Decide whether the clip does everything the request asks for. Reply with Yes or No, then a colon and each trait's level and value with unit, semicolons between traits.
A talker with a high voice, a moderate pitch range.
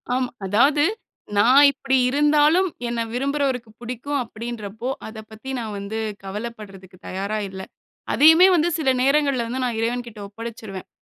Yes: high, 240 Hz; average, 4.5 semitones